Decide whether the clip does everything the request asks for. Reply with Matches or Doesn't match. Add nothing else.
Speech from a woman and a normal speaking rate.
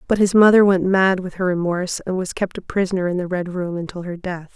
Doesn't match